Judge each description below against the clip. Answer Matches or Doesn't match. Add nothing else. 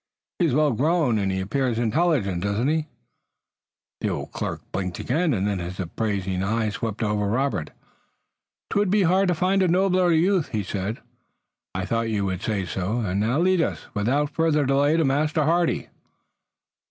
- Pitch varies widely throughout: Matches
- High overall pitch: Doesn't match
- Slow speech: Doesn't match